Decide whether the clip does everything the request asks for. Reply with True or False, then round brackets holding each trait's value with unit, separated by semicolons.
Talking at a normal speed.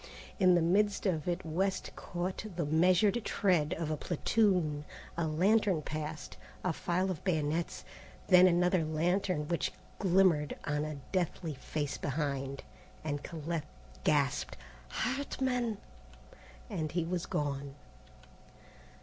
False (120 wpm)